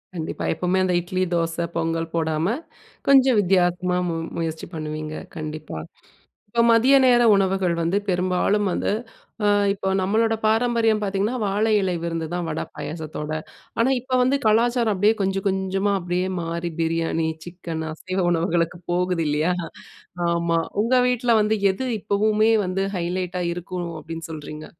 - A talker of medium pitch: Yes, medium, 180 Hz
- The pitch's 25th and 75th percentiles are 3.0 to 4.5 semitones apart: Yes, average, 4.0 semitones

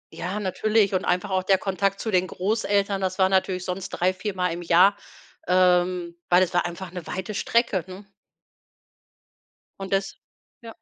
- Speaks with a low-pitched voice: No, medium, 185 Hz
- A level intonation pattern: Yes, narrow, 1.5 semitones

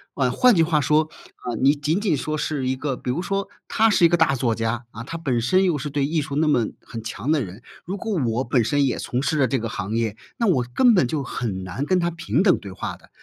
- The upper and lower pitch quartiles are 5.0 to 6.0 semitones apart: Yes, wide, 5.5 semitones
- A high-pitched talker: No, medium, 140 Hz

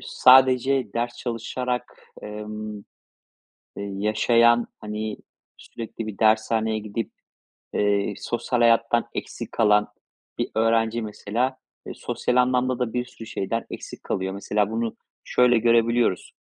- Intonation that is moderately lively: No, narrow, 2.2 semitones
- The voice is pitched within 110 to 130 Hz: Yes, low, 115 Hz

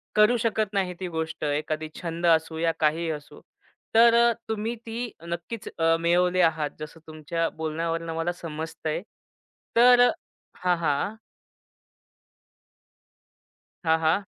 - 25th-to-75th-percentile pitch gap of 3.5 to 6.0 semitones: Yes, average, 4.1 semitones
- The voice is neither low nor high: Yes, medium, 165 Hz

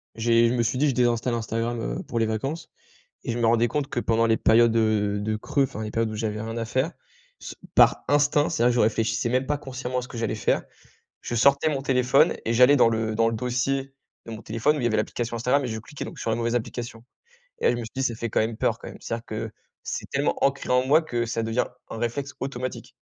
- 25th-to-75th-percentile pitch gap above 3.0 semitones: No, narrow, 2.5 semitones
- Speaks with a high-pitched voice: No, low, 120 Hz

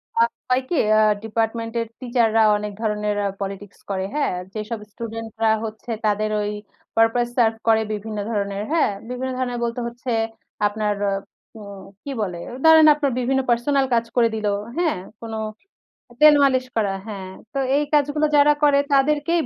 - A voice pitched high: Yes, high, 230 Hz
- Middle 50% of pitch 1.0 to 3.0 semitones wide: No, average, 4.1 semitones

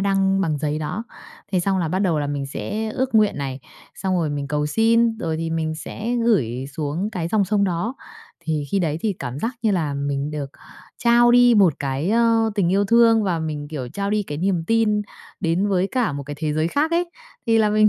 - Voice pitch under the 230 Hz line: Yes, medium, 185 Hz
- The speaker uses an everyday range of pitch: No, wide, 6.3 semitones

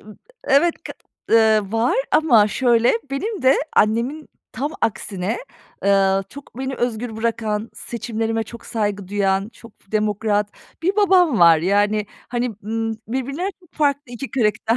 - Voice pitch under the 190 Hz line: No, high, 225 Hz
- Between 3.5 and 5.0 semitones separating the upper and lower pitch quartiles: Yes, average, 3.9 semitones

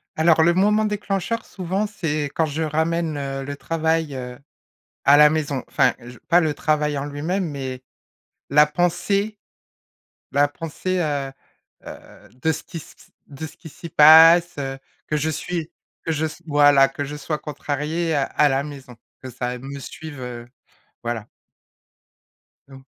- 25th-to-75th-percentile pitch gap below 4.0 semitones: Yes, average, 2.9 semitones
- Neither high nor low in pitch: Yes, medium, 150 Hz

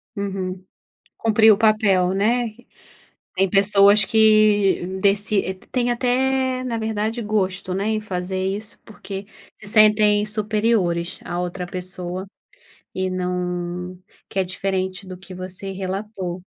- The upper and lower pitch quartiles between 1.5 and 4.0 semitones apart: Yes, average, 2.7 semitones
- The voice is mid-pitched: No, high, 195 Hz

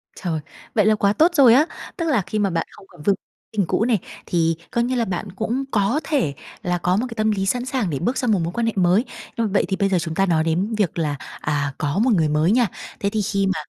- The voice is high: Yes, high, 200 Hz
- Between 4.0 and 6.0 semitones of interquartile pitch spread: Yes, average, 4.7 semitones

